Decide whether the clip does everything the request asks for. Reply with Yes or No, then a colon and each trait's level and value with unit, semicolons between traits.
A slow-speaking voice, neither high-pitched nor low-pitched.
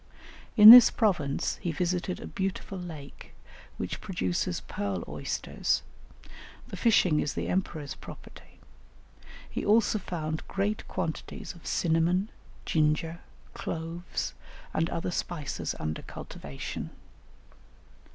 Yes: slow, 105 wpm; medium, 170 Hz